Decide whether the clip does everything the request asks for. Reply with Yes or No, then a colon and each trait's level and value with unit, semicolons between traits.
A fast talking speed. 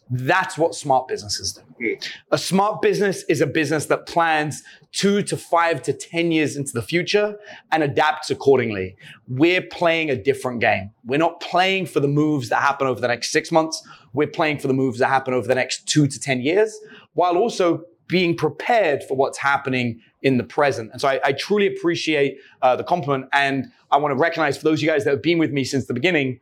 Yes: fast, 215 wpm